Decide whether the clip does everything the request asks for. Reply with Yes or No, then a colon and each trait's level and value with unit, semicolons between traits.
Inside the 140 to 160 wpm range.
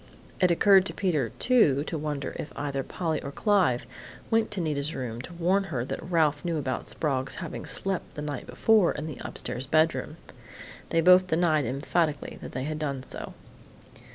No: average, 180 wpm